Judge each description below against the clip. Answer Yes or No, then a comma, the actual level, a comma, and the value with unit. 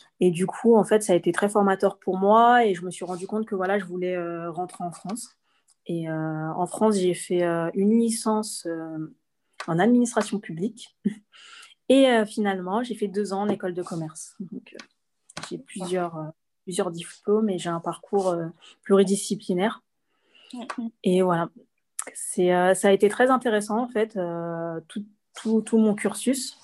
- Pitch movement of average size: Yes, average, 3.5 semitones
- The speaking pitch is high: Yes, high, 195 Hz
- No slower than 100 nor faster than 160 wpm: No, average, 180 wpm